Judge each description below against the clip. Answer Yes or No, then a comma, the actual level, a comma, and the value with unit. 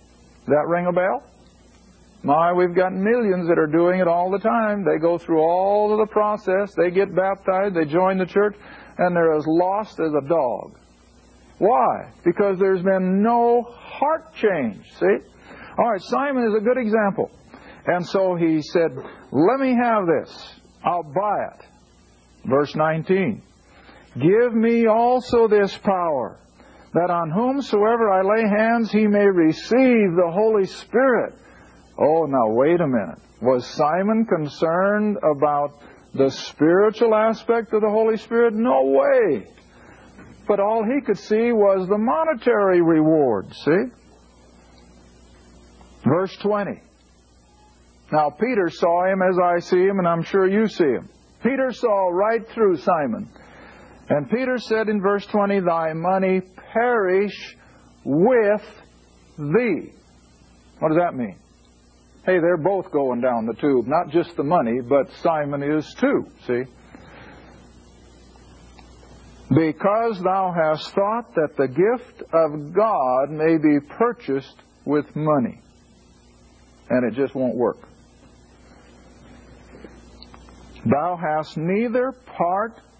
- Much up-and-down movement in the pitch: Yes, wide, 9.0 semitones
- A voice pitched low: No, medium, 175 Hz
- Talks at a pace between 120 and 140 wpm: Yes, slow, 135 wpm